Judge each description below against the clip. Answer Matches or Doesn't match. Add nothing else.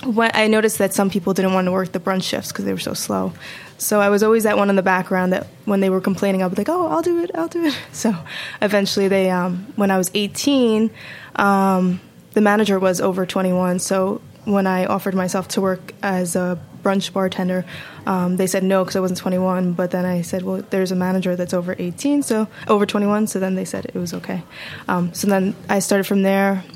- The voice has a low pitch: Doesn't match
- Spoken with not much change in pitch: Matches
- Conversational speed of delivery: Doesn't match